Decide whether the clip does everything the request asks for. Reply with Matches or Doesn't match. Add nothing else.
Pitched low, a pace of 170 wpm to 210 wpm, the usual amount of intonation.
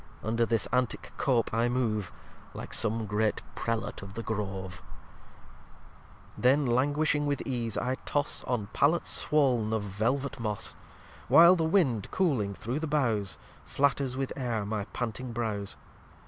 Doesn't match